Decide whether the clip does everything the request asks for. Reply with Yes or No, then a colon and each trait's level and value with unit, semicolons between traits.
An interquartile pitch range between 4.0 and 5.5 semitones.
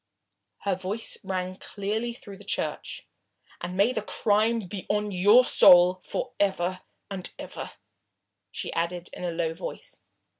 No: narrow, 2.5 semitones